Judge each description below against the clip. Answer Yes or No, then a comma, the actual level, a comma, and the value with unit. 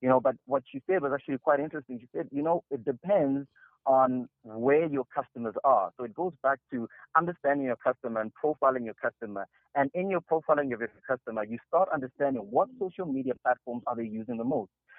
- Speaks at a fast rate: Yes, fast, 210 wpm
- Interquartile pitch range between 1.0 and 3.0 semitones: No, average, 3.5 semitones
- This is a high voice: No, low, 135 Hz